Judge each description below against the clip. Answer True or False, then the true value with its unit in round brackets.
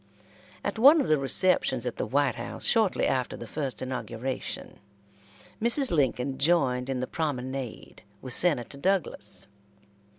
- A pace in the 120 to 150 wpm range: True (135 wpm)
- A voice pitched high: False (135 Hz)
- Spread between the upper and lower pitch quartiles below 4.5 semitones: False (5.3 semitones)